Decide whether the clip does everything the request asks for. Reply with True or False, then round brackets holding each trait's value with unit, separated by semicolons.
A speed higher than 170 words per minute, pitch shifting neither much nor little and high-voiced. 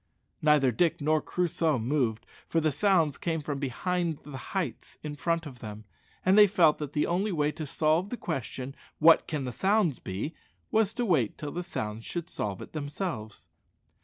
False (185 wpm; 4.4 semitones; 155 Hz)